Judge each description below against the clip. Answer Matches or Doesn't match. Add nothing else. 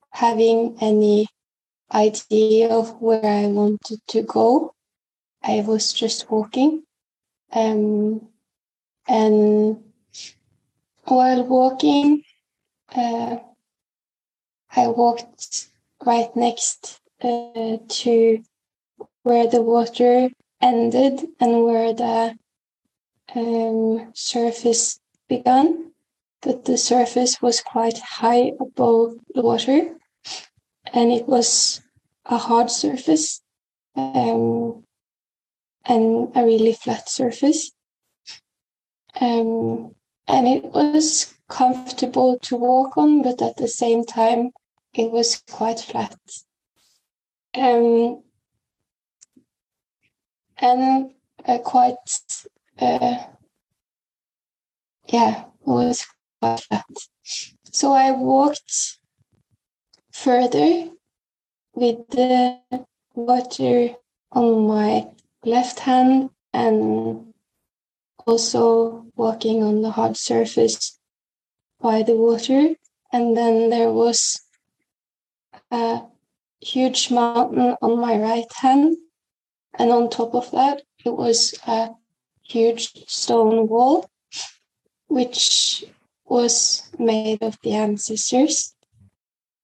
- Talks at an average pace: Doesn't match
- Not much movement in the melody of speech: Matches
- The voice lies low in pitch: Doesn't match